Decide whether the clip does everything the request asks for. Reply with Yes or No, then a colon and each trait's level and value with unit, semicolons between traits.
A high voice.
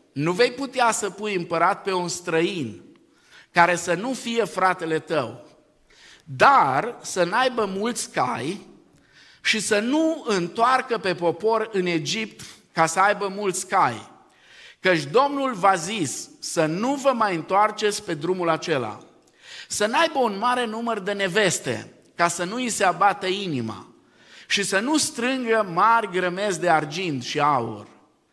Yes: high, 200 Hz